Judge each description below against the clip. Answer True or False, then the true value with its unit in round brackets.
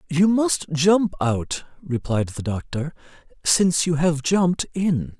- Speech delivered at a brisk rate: False (140 wpm)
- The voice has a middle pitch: True (160 Hz)